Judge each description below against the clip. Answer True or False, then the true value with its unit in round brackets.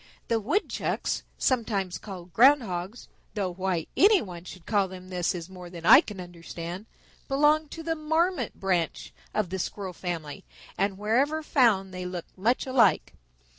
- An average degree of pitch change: False (6.2 semitones)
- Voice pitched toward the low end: False (195 Hz)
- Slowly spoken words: False (160 wpm)